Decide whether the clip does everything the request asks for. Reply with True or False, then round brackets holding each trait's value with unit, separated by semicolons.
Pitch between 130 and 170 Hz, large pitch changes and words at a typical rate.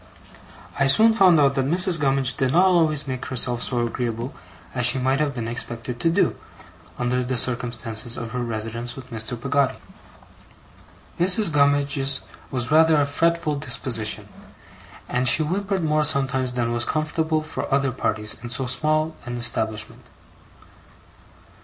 False (135 Hz; 4.2 semitones; 150 wpm)